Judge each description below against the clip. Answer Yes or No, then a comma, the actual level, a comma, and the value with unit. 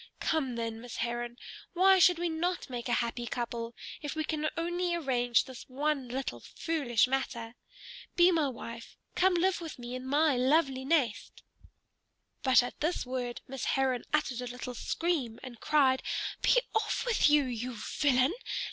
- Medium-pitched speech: No, very high, 265 Hz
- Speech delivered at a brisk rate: No, average, 165 wpm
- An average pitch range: Yes, average, 4.8 semitones